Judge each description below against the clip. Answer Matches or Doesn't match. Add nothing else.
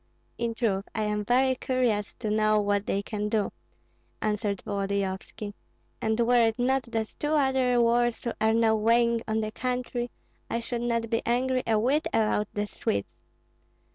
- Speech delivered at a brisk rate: Doesn't match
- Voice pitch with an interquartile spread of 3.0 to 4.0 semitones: Doesn't match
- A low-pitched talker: Doesn't match